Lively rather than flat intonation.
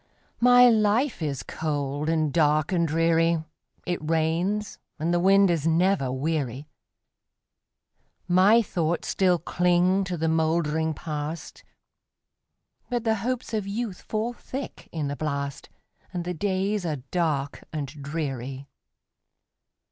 No: average, 4.2 semitones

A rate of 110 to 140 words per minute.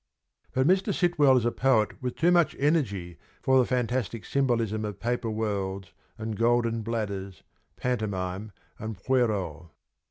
Yes: slow, 135 wpm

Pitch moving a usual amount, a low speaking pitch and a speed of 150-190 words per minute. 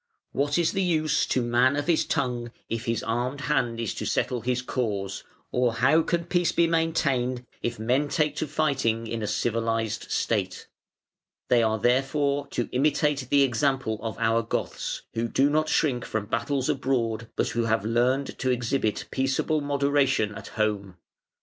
Yes: average, 3.8 semitones; low, 125 Hz; average, 170 wpm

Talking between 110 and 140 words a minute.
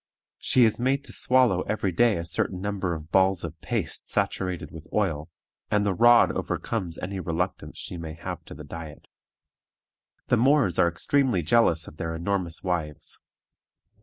No: average, 165 wpm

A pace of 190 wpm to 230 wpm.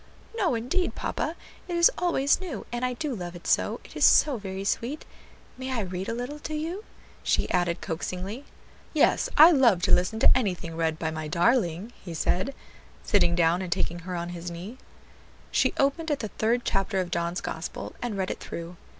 Yes: average, 195 wpm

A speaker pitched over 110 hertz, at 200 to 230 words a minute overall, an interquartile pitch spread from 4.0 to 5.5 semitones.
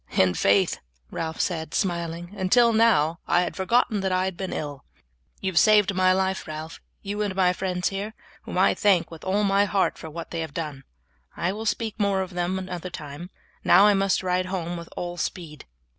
No: medium, 185 Hz; fast, 205 wpm; average, 2.8 semitones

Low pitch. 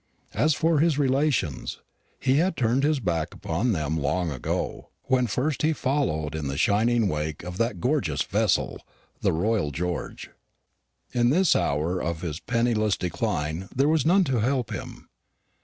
Yes: low, 110 Hz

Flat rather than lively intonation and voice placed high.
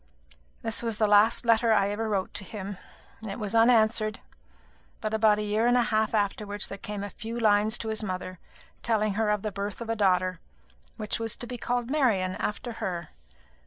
Yes: narrow, 1.9 semitones; high, 215 Hz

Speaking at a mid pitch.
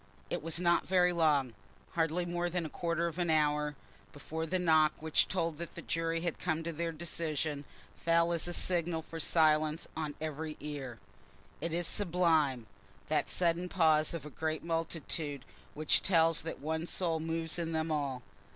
Yes: medium, 160 Hz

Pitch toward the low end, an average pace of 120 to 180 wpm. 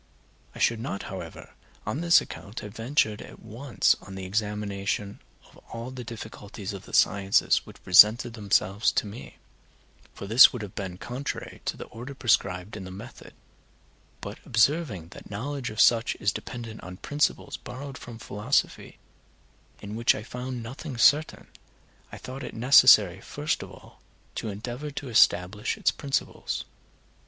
Yes: low, 110 Hz; average, 160 wpm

